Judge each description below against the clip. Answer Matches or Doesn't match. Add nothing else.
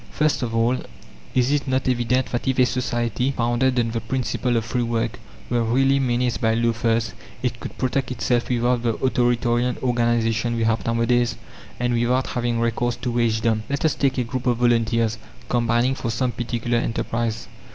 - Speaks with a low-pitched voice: Matches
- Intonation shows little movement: Matches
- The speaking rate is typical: Matches